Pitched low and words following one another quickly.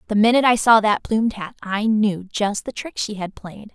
No: high, 215 Hz; fast, 240 wpm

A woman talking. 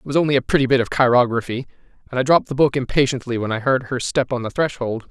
No: male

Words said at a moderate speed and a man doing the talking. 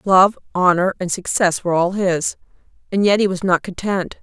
No: average, 185 wpm; female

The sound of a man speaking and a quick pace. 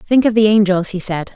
No: female; fast, 265 wpm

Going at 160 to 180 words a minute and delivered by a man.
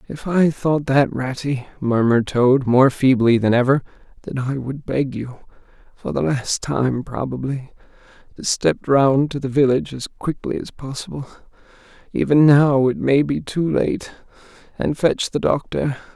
No: average, 140 wpm; male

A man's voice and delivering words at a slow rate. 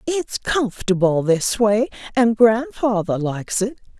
No: female; slow, 120 wpm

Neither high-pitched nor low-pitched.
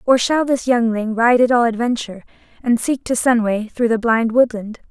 No: high, 235 Hz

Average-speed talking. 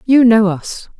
Yes: average, 180 wpm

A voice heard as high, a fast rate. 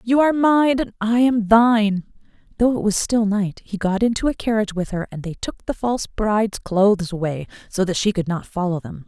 Yes: high, 210 Hz; fast, 225 wpm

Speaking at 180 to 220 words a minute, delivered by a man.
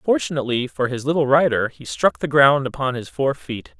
Yes: fast, 205 wpm; male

